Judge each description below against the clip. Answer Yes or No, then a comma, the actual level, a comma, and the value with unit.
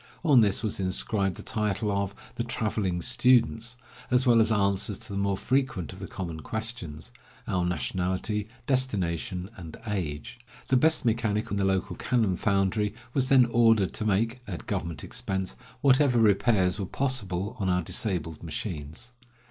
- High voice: No, low, 100 Hz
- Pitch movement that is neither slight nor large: Yes, average, 3.9 semitones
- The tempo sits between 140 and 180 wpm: Yes, average, 160 wpm